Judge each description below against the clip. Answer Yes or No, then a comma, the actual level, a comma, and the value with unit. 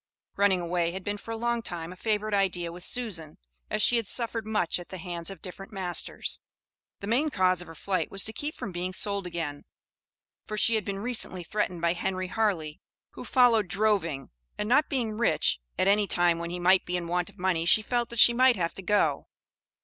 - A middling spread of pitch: Yes, average, 3.7 semitones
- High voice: Yes, high, 195 Hz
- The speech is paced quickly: Yes, fast, 220 wpm